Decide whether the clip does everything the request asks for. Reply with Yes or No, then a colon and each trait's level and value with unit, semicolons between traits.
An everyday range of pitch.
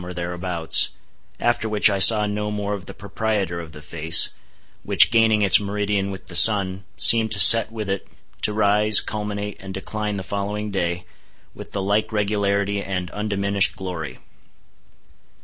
No: narrow, 1.8 semitones